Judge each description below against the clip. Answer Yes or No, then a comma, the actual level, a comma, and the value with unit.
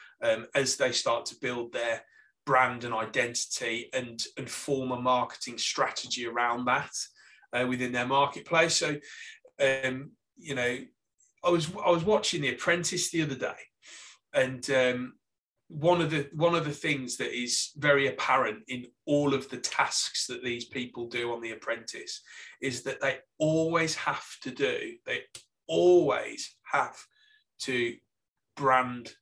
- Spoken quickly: No, average, 150 wpm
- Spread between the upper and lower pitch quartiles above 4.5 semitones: Yes, average, 5.1 semitones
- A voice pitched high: No, low, 135 Hz